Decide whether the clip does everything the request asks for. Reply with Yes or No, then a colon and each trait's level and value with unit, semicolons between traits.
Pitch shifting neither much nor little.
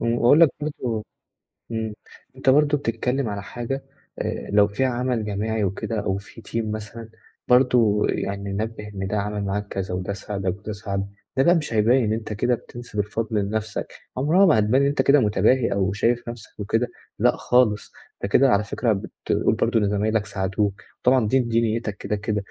Yes: average, 3.1 semitones